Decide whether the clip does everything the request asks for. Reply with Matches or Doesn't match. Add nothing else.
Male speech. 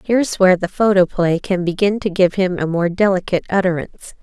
Doesn't match